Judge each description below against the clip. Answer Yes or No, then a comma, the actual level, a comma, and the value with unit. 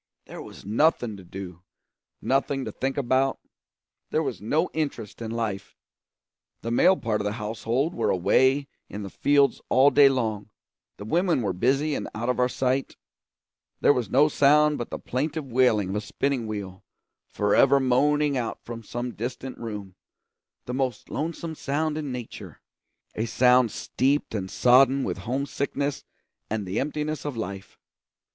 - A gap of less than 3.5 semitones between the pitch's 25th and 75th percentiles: No, average, 4.3 semitones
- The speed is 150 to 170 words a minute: Yes, average, 155 wpm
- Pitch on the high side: No, low, 125 Hz